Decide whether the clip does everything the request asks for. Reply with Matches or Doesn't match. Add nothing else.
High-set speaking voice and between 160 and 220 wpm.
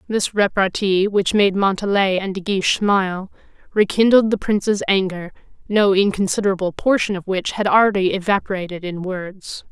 Doesn't match